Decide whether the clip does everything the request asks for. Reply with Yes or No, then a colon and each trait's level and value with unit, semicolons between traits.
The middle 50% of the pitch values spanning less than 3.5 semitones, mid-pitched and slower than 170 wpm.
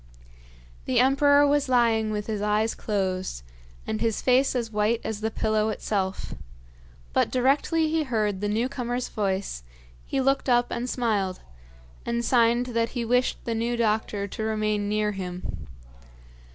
No: average, 3.0 semitones; high, 225 Hz; average, 150 wpm